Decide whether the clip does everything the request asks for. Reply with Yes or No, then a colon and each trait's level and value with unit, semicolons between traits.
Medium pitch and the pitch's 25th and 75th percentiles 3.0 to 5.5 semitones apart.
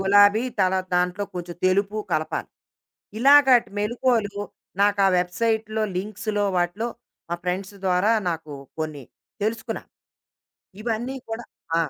No: high, 205 Hz; average, 3.5 semitones